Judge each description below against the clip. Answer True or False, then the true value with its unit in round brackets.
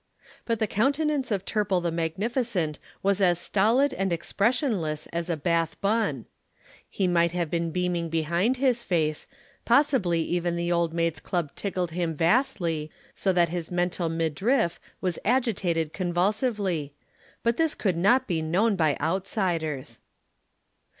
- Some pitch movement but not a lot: True (4.3 semitones)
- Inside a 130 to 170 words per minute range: True (140 wpm)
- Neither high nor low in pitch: True (175 Hz)